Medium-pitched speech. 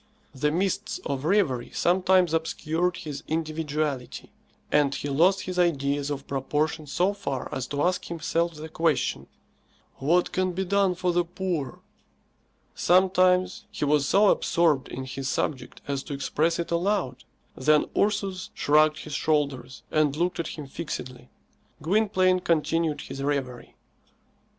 Yes: medium, 160 Hz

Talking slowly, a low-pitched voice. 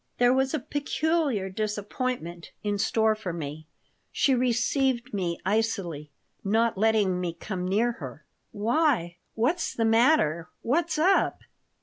No: slow, 125 wpm; high, 220 Hz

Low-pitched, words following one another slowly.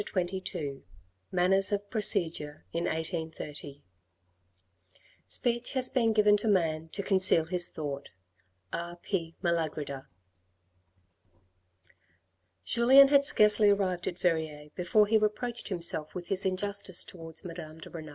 No: medium, 180 Hz; slow, 120 wpm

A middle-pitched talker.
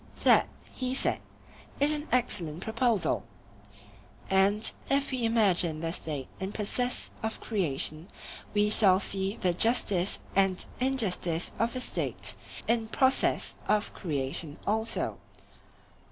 No: high, 205 Hz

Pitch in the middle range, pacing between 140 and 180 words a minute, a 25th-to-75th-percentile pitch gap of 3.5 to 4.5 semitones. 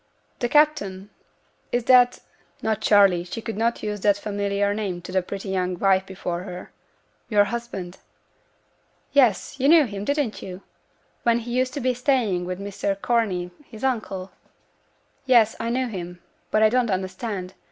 No: high, 205 Hz; average, 160 wpm; average, 4.1 semitones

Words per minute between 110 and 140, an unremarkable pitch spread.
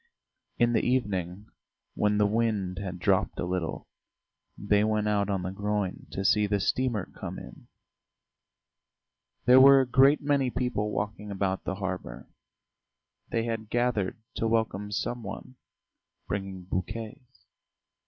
Yes: slow, 135 wpm; average, 3.5 semitones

